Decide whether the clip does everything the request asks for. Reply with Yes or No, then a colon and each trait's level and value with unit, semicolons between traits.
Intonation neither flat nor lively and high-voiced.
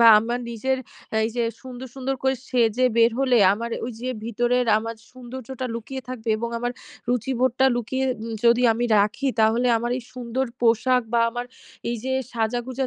No: narrow, 1.9 semitones; high, 245 Hz